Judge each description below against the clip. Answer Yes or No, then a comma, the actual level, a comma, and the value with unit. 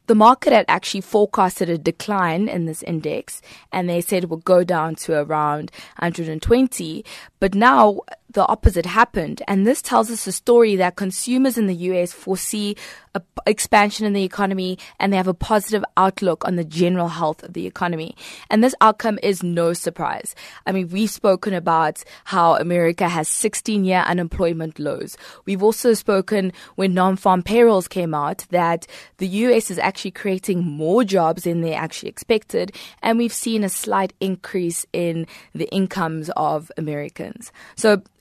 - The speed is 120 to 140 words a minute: No, average, 170 wpm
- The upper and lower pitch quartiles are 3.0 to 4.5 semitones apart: Yes, average, 3.7 semitones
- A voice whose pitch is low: No, high, 190 Hz